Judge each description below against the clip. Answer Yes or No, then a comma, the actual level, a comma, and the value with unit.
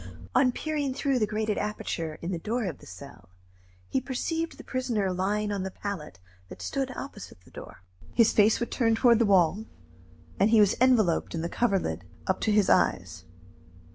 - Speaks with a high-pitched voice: Yes, high, 210 Hz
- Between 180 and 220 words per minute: Yes, average, 185 wpm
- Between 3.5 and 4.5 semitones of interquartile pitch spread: No, average, 5.1 semitones